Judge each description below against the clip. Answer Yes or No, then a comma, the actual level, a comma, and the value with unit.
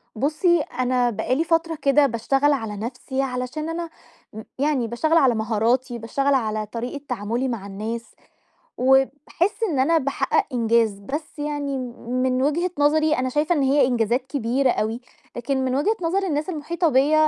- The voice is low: No, very high, 265 Hz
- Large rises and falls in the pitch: No, average, 4.0 semitones